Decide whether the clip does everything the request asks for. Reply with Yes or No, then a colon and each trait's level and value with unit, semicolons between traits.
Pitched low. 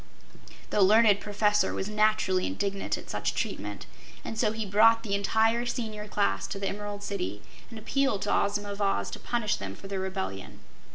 No: high, 205 Hz